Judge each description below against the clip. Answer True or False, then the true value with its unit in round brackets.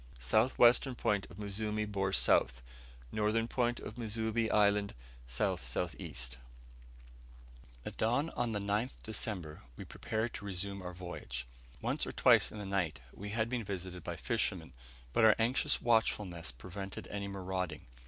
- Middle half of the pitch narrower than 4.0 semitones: True (3.4 semitones)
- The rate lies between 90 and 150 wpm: True (145 wpm)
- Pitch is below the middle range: True (100 Hz)